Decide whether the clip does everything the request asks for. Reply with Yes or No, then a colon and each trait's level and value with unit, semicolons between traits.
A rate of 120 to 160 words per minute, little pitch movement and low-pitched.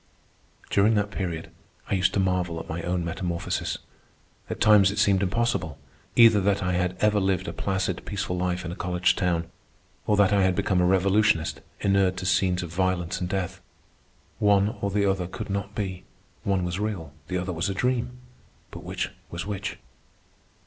No: average, 185 wpm; narrow, 2.0 semitones; very low, 95 Hz